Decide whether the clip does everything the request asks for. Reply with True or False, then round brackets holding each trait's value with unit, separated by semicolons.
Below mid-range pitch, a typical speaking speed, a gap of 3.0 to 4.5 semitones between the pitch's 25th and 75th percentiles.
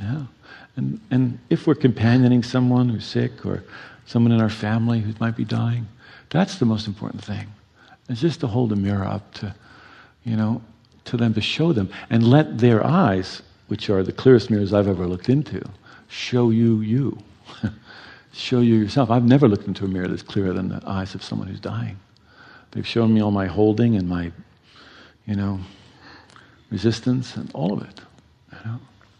True (115 Hz; 185 wpm; 3.4 semitones)